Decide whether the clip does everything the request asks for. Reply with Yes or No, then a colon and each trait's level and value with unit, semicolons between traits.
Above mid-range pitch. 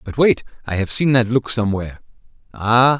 No: low, 115 Hz